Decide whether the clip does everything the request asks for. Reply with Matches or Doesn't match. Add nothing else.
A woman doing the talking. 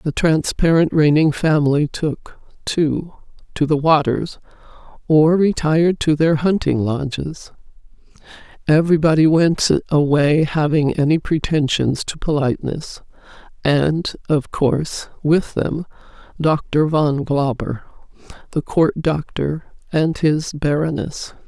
Matches